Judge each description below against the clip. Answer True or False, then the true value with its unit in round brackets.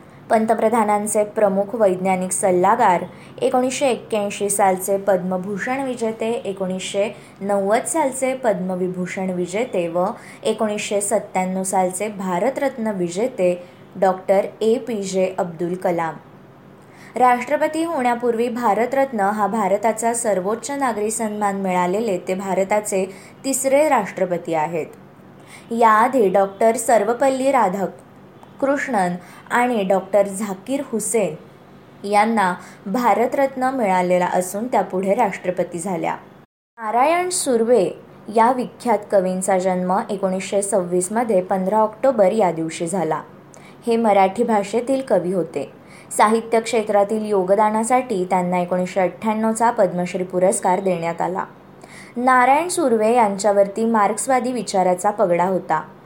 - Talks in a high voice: True (205 Hz)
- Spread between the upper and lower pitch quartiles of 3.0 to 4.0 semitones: True (3.7 semitones)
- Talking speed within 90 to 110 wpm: True (95 wpm)